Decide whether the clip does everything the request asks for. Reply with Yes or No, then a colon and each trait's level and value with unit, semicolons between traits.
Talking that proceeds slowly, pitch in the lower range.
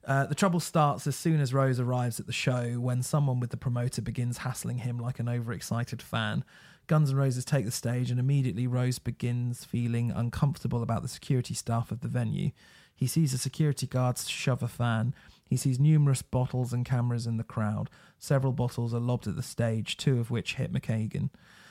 No: average, 200 wpm; low, 125 Hz